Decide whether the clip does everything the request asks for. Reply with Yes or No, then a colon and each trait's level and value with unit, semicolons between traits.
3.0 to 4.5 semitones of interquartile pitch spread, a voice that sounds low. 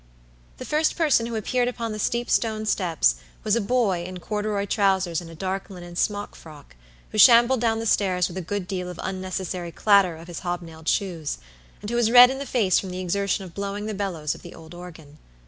No: average, 3.8 semitones; high, 195 Hz